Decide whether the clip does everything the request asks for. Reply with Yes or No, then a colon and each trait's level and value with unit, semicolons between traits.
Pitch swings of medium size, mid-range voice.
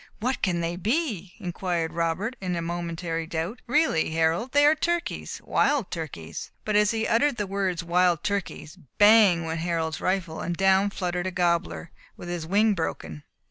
Yes: average, 4.0 semitones; medium, 180 Hz